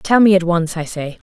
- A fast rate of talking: Yes, fast, 285 wpm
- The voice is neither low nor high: Yes, medium, 180 Hz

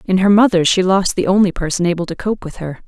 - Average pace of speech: No, fast, 270 wpm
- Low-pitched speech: No, medium, 185 Hz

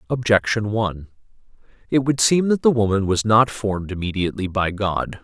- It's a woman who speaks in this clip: No, male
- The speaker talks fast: No, average, 160 wpm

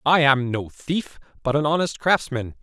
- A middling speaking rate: Yes, average, 185 wpm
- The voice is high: No, medium, 145 Hz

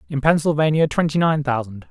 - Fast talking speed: No, average, 155 wpm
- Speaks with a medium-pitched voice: Yes, medium, 145 Hz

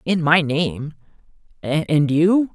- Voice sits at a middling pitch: Yes, medium, 160 Hz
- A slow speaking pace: Yes, slow, 95 wpm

